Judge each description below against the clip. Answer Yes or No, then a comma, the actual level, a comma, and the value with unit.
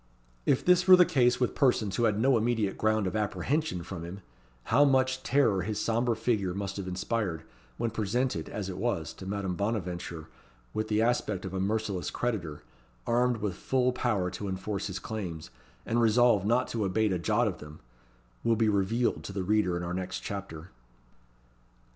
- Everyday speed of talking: Yes, average, 185 wpm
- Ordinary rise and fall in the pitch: Yes, average, 4.2 semitones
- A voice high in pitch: No, low, 105 Hz